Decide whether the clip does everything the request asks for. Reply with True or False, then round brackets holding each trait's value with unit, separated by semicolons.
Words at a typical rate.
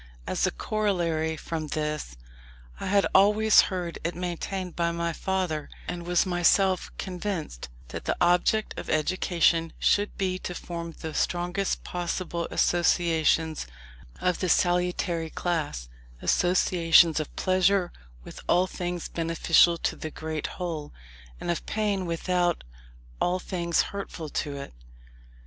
False (130 wpm)